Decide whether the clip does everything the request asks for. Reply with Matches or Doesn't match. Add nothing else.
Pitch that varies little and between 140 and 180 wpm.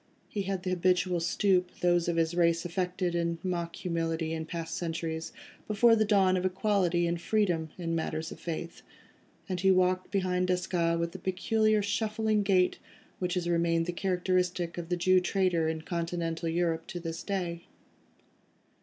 Matches